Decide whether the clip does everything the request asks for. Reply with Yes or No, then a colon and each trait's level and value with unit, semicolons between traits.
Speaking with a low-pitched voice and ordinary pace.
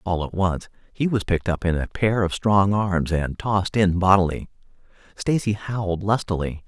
Yes: very low, 95 Hz; average, 180 wpm